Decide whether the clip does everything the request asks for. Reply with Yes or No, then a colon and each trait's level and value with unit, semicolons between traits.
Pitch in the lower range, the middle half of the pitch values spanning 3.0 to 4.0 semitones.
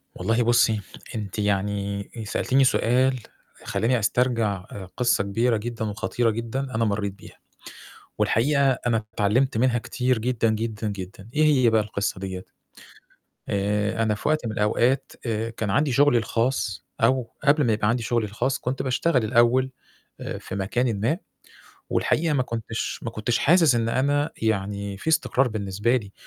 Yes: low, 115 Hz; average, 3.5 semitones